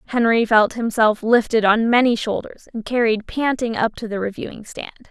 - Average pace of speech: Yes, average, 175 wpm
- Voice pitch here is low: No, high, 225 Hz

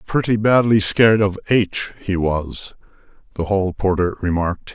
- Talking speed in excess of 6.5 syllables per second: No, 4.2 syllables/s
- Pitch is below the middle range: Yes, low, 100 Hz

